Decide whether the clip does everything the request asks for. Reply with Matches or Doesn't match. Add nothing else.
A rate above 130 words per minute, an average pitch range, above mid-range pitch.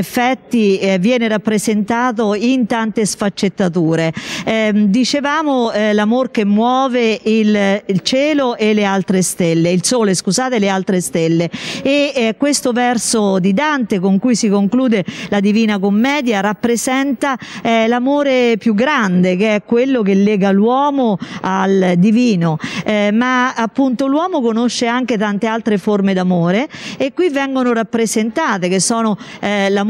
Matches